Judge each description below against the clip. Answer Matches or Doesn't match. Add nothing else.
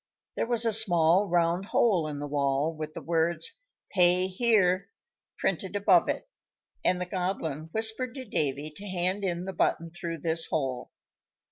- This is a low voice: Doesn't match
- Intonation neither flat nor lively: Matches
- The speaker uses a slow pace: Doesn't match